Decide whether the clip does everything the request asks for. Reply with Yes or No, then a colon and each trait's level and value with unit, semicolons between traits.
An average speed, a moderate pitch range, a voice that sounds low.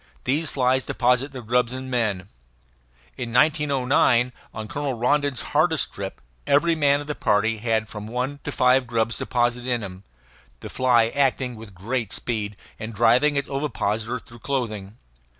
Yes: average, 155 wpm; average, 3.5 semitones; low, 125 Hz